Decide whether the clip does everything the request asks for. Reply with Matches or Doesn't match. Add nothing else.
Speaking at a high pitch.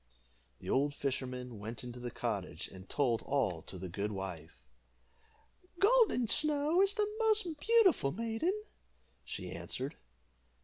Doesn't match